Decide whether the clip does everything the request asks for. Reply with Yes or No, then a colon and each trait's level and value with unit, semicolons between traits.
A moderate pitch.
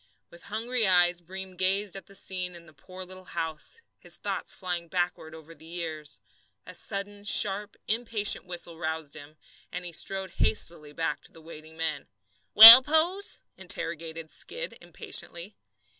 Yes: medium, 180 Hz